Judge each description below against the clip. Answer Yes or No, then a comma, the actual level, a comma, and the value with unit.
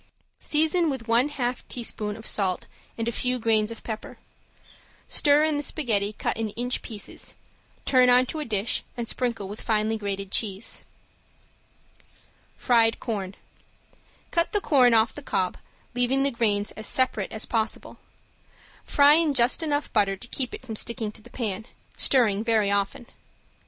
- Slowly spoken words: No, average, 160 wpm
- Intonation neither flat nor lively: Yes, average, 3.4 semitones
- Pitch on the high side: Yes, high, 230 Hz